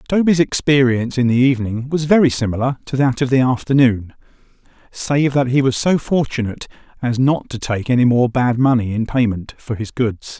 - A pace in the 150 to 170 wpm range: No, average, 185 wpm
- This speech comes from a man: Yes, male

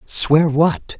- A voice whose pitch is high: No, medium, 150 Hz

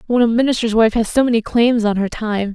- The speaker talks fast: Yes, fast, 260 wpm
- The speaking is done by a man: No, female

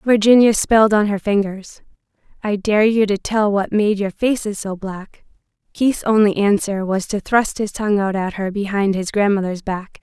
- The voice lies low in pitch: No, high, 205 Hz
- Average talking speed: Yes, average, 185 wpm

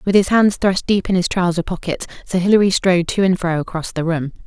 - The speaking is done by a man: No, female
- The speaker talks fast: Yes, fast, 240 wpm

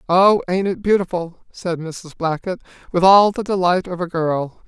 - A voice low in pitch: No, medium, 180 Hz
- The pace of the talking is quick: No, average, 180 wpm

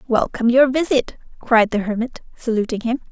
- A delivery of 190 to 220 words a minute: No, average, 155 wpm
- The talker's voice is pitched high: Yes, high, 240 Hz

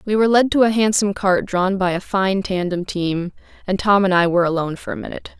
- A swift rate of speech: Yes, fast, 245 wpm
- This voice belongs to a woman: Yes, female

